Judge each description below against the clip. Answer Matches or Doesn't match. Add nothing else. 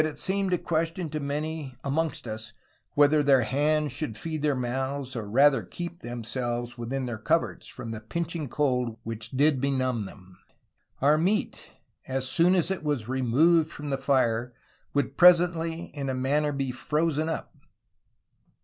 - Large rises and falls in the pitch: Doesn't match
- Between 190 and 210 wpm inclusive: Doesn't match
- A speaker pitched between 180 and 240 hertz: Doesn't match